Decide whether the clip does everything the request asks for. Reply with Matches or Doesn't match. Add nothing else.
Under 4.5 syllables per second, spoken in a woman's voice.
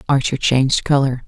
Doesn't match